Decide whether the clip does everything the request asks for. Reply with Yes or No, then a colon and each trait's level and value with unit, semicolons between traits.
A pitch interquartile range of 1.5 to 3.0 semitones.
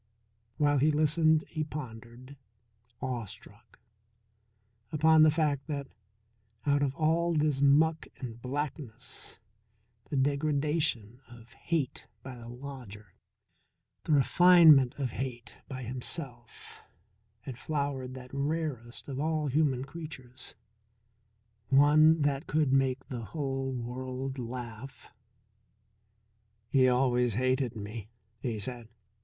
No: average, 3.4 semitones